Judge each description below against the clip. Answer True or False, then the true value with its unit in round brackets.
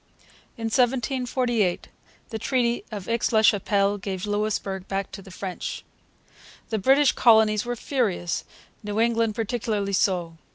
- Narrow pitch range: False (3.1 semitones)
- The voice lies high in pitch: True (215 Hz)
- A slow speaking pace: True (130 wpm)